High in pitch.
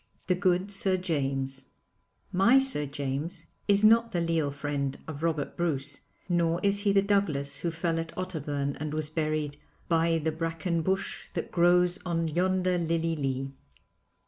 No: medium, 165 Hz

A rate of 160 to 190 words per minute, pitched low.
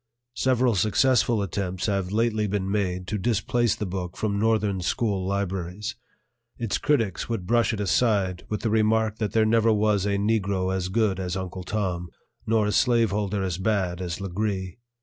Yes: average, 170 wpm; low, 105 Hz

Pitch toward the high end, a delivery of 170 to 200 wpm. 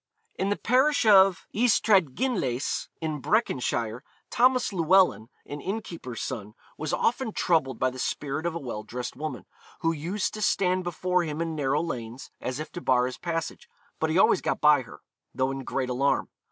No: medium, 160 Hz; average, 175 wpm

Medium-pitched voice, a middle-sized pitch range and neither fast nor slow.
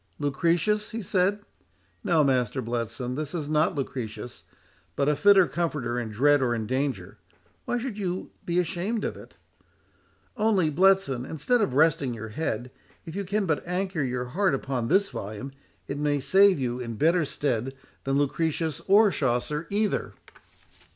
No: medium, 150 Hz; wide, 6.7 semitones; average, 155 wpm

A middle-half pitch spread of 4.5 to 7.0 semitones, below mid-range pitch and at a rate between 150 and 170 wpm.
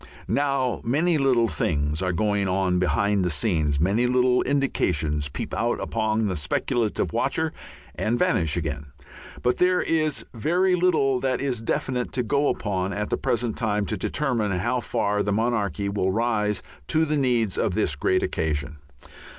Yes: wide, 5.6 semitones; low, 110 Hz; average, 160 wpm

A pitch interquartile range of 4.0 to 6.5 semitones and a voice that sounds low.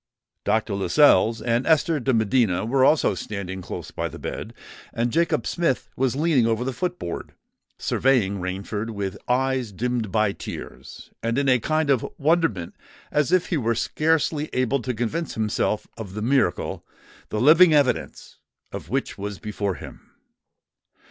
Yes: average, 5.3 semitones; low, 120 Hz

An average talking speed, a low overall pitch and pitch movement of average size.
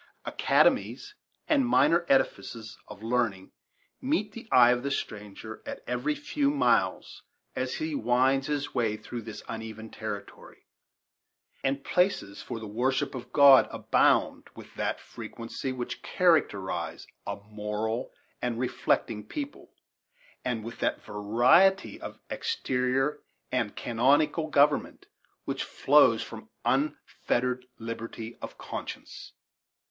No: slow, 120 wpm; low, 125 Hz; average, 5.0 semitones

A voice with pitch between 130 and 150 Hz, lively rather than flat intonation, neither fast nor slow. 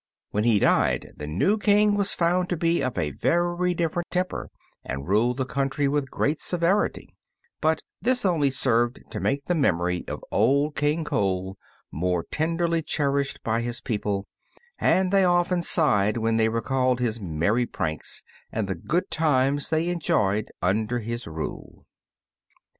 Yes: low, 135 Hz; wide, 7.9 semitones; average, 155 wpm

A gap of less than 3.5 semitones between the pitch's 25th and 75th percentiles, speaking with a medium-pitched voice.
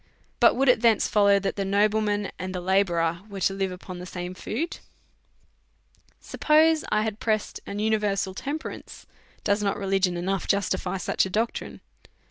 No: narrow, 2.4 semitones; high, 200 Hz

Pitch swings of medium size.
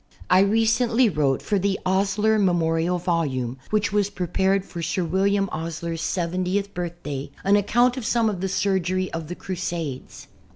Yes: average, 3.3 semitones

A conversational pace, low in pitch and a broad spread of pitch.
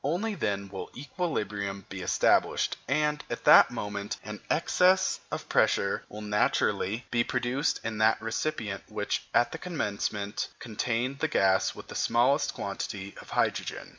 Yes: average, 145 wpm; low, 115 Hz; wide, 5.7 semitones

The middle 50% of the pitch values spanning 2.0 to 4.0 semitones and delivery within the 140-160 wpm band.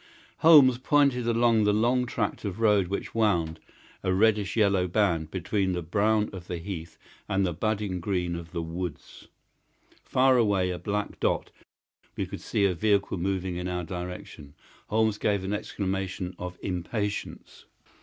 Yes: average, 3.3 semitones; average, 155 wpm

